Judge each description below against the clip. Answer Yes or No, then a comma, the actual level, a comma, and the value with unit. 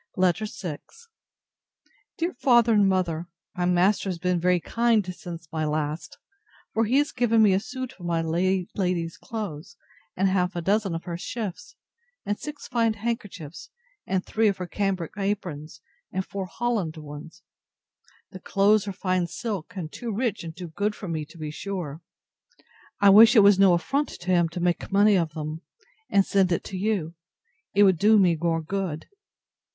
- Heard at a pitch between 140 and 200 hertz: Yes, medium, 185 Hz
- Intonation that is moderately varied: Yes, average, 3.7 semitones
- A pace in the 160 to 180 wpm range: Yes, average, 175 wpm